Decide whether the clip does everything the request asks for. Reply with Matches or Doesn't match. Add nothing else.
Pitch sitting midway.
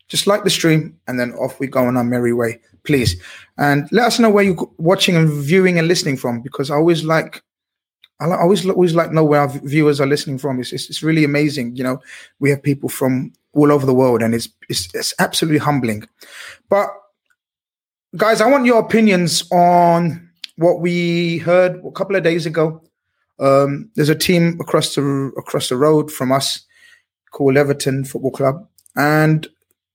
Matches